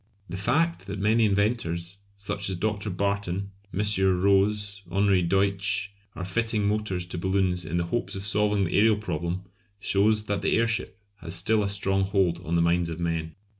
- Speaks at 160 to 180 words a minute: Yes, average, 175 wpm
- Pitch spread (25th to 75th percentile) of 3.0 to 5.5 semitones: No, narrow, 2.6 semitones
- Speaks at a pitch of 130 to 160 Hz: No, low, 100 Hz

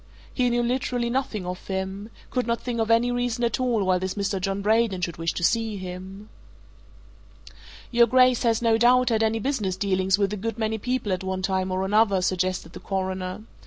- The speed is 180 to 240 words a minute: Yes, average, 200 wpm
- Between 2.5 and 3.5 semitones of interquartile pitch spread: No, average, 3.9 semitones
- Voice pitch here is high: Yes, high, 210 Hz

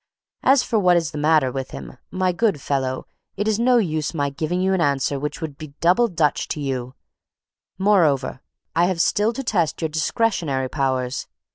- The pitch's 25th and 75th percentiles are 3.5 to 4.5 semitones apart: No, average, 5.3 semitones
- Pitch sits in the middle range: Yes, medium, 160 Hz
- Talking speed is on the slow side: No, average, 185 wpm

